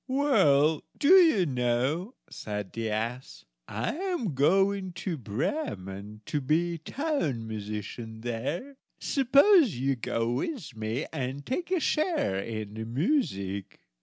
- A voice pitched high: No, medium, 140 Hz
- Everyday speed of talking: No, slow, 125 wpm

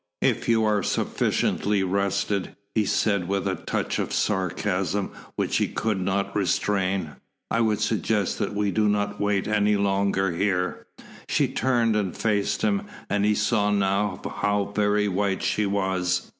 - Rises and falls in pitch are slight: Yes, narrow, 1.5 semitones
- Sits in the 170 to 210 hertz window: No, low, 100 Hz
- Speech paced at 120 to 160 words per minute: Yes, average, 155 wpm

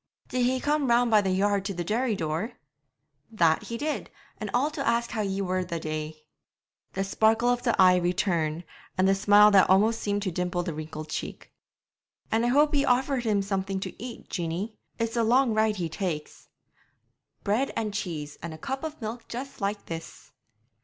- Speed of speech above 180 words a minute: Yes, average, 195 wpm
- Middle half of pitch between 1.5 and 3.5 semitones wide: No, average, 4.8 semitones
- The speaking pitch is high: Yes, high, 205 Hz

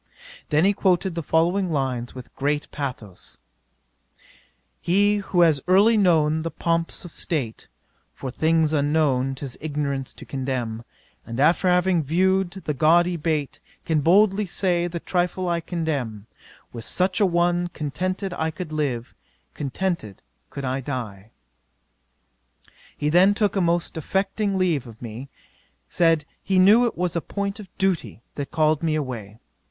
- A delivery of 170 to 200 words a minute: No, average, 145 wpm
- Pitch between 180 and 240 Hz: No, medium, 160 Hz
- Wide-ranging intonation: No, average, 4.8 semitones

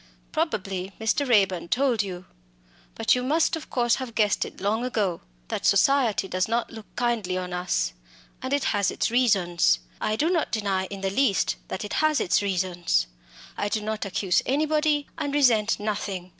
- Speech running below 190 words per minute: Yes, average, 170 wpm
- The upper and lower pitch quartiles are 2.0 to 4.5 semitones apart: No, average, 5.3 semitones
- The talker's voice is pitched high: Yes, high, 215 Hz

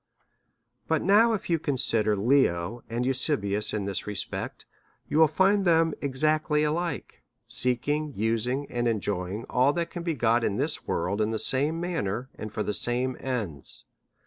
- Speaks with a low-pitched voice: Yes, low, 125 Hz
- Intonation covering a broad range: Yes, wide, 6.2 semitones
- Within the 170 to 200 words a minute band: No, average, 160 wpm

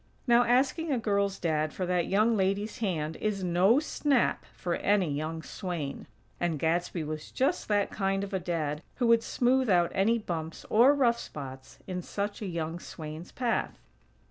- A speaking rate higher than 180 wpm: No, average, 170 wpm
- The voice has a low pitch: No, high, 190 Hz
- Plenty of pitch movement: Yes, wide, 5.8 semitones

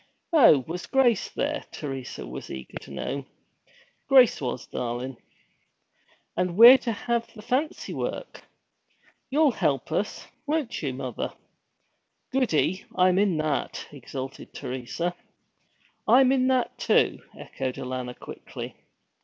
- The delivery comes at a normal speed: No, slow, 120 wpm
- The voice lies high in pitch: No, medium, 180 Hz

